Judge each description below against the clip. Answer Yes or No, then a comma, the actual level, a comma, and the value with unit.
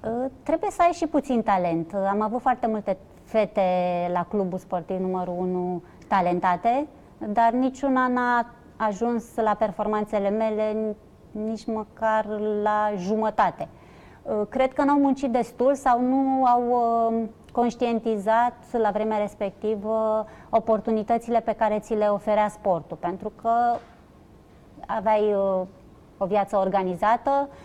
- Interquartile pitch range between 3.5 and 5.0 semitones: No, average, 2.9 semitones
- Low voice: No, high, 220 Hz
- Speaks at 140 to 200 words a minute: No, slow, 115 wpm